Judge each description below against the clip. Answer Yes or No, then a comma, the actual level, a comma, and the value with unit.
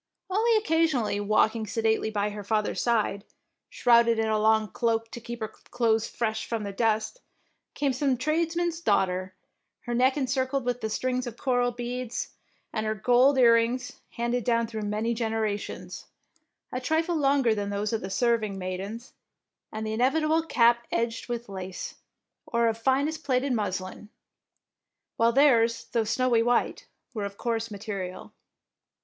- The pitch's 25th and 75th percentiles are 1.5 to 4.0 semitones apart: Yes, average, 2.7 semitones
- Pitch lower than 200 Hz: No, high, 230 Hz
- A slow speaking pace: No, average, 150 wpm